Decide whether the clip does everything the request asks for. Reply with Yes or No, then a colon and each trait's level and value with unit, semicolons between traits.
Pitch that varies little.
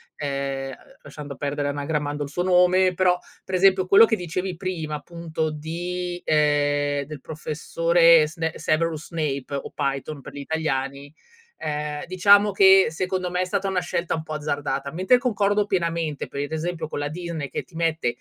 No: average, 3.7 semitones